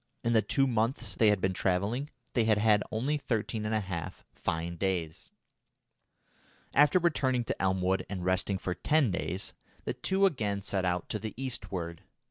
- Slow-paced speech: No, average, 170 wpm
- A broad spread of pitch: No, average, 4.8 semitones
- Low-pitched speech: Yes, low, 105 Hz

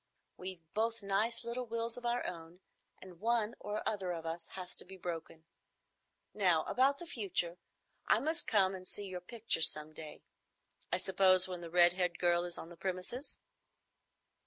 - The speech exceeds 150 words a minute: Yes, average, 170 wpm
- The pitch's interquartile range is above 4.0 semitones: Yes, average, 4.4 semitones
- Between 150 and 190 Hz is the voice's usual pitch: Yes, medium, 185 Hz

